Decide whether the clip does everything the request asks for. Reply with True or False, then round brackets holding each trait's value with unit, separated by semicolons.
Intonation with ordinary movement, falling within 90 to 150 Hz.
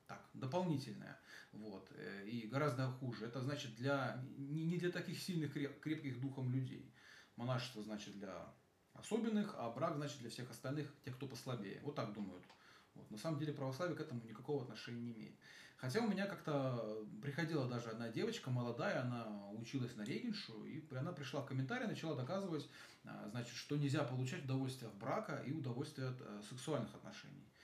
True (4.1 semitones; 135 Hz)